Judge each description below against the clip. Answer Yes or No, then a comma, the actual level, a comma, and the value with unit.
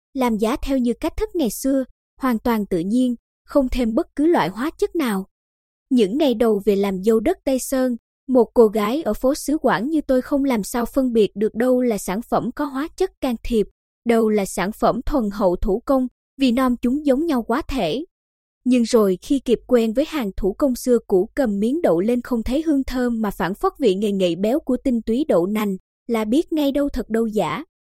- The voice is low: No, high, 245 Hz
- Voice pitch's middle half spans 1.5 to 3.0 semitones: No, average, 4.0 semitones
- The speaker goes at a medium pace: Yes, average, 230 wpm